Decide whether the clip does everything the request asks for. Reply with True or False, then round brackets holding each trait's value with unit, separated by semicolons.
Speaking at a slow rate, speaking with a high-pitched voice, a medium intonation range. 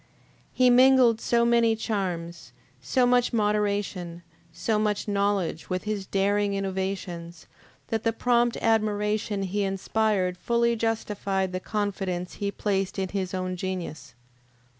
True (125 wpm; 205 Hz; 3.1 semitones)